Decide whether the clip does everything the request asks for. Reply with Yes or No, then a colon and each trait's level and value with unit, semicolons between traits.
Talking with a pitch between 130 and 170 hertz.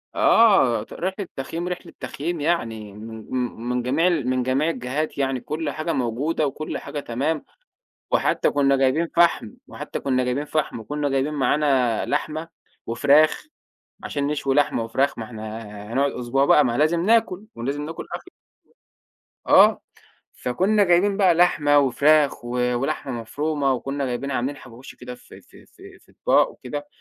Yes: medium, 140 Hz